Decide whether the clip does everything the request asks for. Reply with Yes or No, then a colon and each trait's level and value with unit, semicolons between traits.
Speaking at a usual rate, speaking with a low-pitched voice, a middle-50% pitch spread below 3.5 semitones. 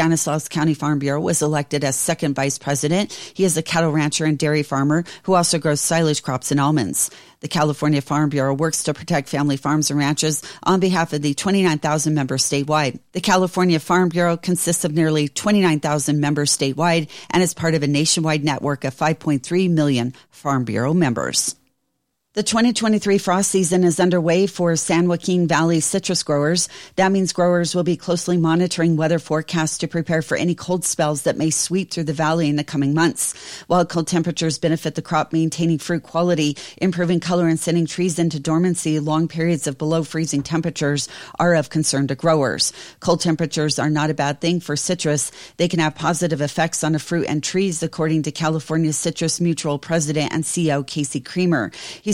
No: average, 185 wpm; medium, 160 Hz; narrow, 2.5 semitones